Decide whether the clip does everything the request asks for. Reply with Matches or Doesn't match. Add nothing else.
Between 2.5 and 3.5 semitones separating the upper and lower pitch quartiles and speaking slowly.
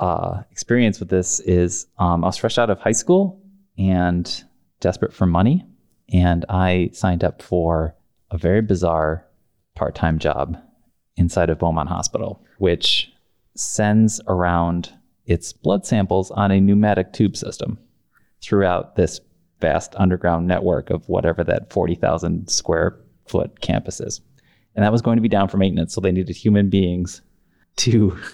Doesn't match